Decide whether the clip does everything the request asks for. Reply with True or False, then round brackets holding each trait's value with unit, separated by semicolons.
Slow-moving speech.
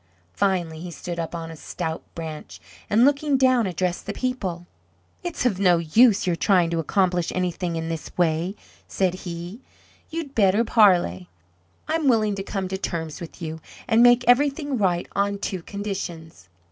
False (165 wpm)